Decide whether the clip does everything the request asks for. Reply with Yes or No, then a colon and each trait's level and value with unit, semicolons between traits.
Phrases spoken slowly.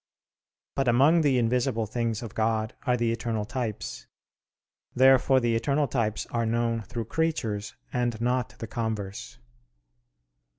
Yes: slow, 130 wpm